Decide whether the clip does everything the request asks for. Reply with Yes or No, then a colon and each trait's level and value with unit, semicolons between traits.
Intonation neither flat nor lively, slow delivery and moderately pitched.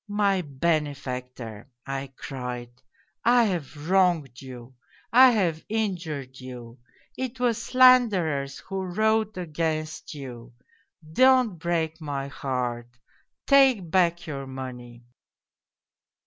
No: wide, 6.8 semitones; slow, 105 wpm; medium, 155 Hz